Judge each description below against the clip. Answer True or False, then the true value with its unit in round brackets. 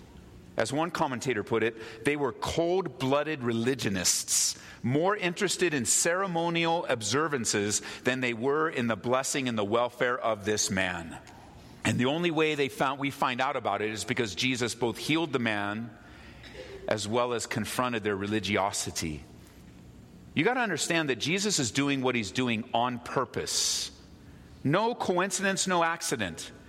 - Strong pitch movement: True (5.8 semitones)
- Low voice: True (120 Hz)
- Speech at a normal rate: True (150 wpm)